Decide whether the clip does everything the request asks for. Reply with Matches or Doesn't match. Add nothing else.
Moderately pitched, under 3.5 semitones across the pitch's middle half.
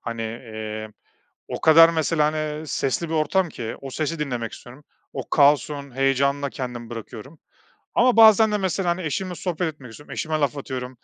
Doesn't match